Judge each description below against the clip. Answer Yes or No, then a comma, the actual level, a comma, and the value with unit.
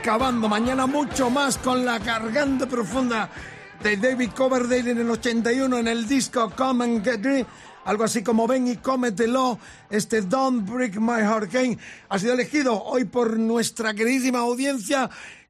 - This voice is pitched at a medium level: No, high, 245 Hz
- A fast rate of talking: No, average, 160 wpm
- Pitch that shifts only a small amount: Yes, narrow, 2.2 semitones